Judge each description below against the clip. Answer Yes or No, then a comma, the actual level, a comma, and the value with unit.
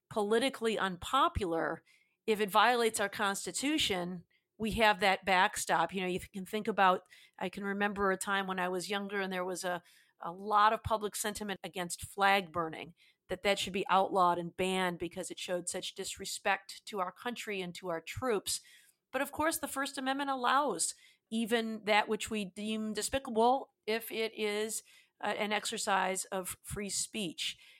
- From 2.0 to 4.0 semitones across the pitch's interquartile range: Yes, average, 2.9 semitones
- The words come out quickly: No, average, 170 wpm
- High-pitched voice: Yes, high, 200 Hz